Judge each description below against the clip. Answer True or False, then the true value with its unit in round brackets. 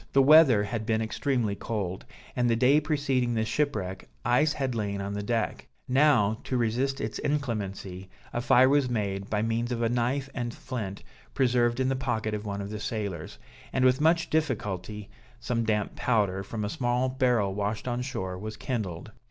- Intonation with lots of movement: False (3.9 semitones)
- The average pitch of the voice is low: True (115 Hz)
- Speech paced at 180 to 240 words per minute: True (185 wpm)